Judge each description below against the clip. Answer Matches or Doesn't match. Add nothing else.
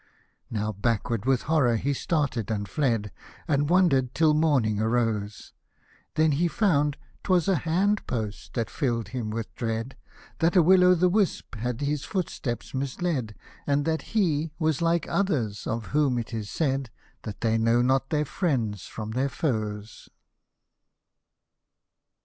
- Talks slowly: Doesn't match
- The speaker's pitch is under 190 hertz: Matches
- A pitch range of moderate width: Doesn't match